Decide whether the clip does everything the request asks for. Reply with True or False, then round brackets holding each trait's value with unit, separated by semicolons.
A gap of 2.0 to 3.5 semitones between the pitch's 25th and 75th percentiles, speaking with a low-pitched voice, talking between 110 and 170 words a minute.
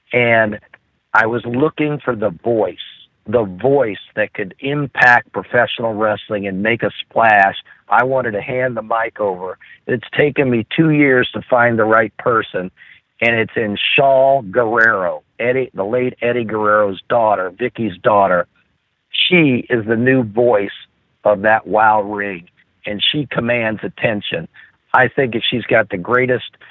True (2.9 semitones; 115 Hz; 155 wpm)